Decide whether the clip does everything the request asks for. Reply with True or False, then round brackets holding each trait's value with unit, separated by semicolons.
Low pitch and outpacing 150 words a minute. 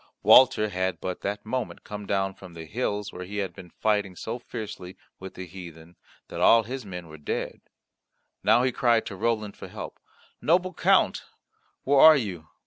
True (100 Hz; 180 wpm)